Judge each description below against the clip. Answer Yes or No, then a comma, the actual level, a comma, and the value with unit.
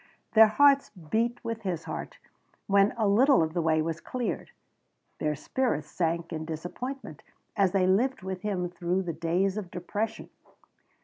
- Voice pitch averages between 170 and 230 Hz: Yes, high, 190 Hz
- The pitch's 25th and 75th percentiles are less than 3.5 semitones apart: No, average, 4.8 semitones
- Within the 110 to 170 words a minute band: Yes, average, 160 wpm